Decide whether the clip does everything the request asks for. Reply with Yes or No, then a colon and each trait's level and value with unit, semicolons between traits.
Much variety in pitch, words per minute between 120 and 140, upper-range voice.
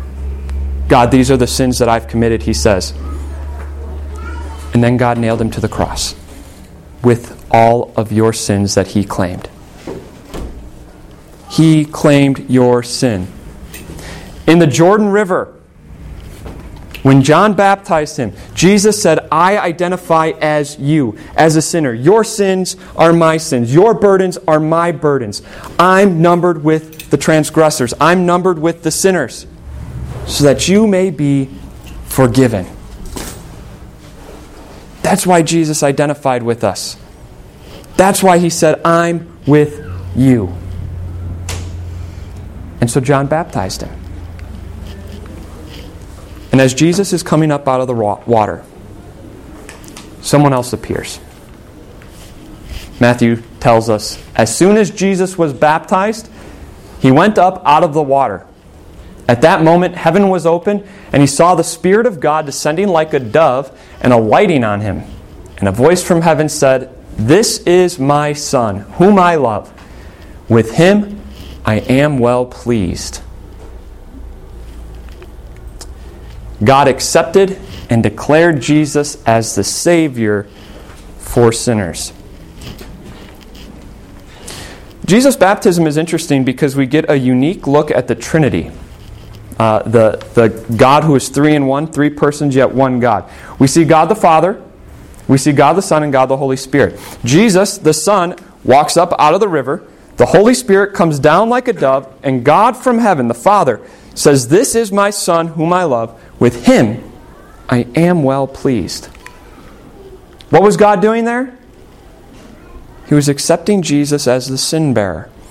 No: wide, 8.9 semitones; slow, 135 wpm; low, 135 Hz